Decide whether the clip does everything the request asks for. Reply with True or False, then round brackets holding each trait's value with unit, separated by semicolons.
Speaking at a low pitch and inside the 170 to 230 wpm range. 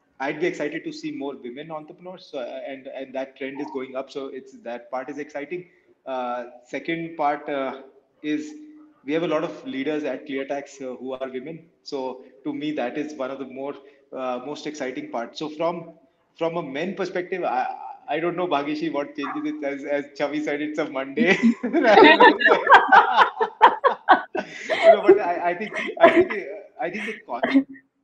False (155 Hz; 195 wpm)